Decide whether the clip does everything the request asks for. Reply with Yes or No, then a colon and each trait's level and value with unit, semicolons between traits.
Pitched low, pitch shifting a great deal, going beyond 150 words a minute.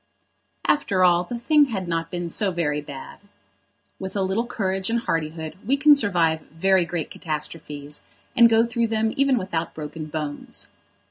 No: medium, 185 Hz; wide, 5.9 semitones; average, 160 wpm